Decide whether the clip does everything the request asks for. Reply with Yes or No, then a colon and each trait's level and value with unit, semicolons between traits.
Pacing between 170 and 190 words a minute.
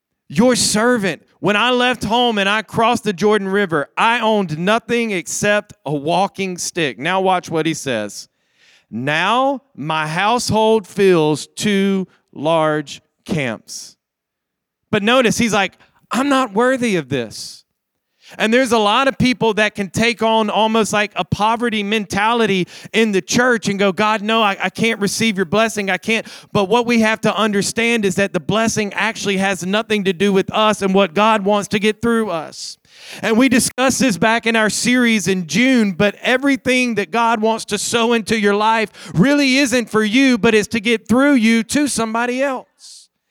Yes: average, 175 wpm